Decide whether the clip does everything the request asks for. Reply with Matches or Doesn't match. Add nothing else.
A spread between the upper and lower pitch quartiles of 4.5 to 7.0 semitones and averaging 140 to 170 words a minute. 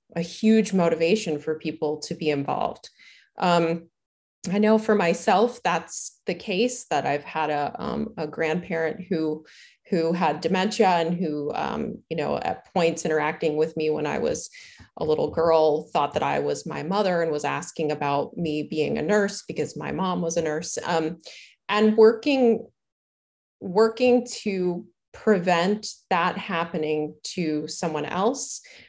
Matches